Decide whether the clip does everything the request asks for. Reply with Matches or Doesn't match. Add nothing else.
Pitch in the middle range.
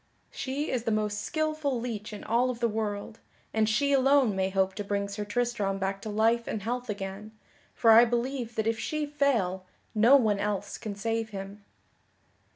Doesn't match